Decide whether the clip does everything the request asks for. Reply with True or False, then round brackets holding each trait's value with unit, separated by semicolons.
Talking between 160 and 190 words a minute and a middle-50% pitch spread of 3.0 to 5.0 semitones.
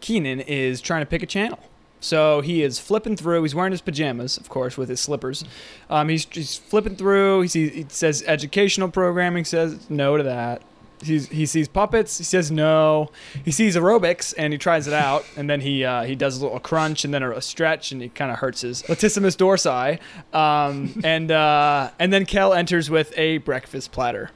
False (205 wpm; 3.7 semitones)